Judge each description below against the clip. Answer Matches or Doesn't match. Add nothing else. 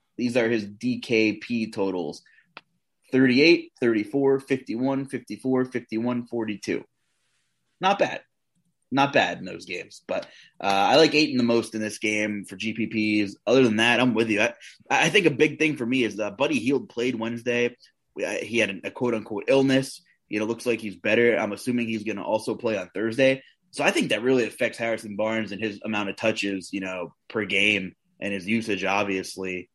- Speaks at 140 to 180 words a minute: Doesn't match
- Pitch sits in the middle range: Doesn't match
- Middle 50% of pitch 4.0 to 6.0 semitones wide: Doesn't match